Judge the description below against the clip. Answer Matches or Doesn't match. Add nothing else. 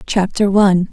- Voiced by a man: Doesn't match